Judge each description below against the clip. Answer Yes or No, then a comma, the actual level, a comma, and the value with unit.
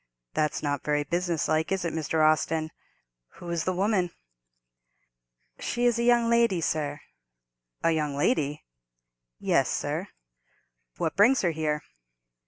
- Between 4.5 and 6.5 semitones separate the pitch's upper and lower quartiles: No, average, 4.1 semitones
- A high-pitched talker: No, medium, 160 Hz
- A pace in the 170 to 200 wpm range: No, slow, 135 wpm